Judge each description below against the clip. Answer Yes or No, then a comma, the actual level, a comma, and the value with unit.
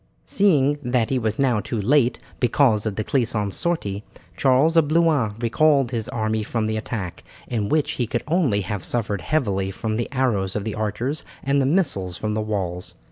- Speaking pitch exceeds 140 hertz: No, low, 115 Hz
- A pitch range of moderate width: Yes, average, 4.7 semitones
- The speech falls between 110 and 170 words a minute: No, average, 190 wpm